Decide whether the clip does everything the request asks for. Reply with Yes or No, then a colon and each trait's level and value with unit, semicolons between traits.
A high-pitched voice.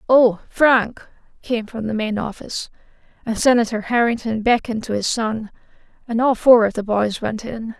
Yes: high, 225 Hz